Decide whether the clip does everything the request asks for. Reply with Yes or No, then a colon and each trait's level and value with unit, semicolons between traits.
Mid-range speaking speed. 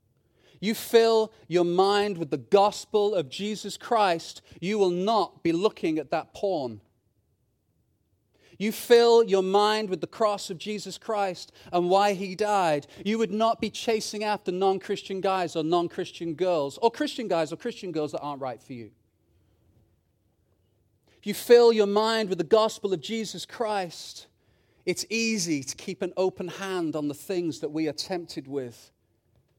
Yes: average, 165 wpm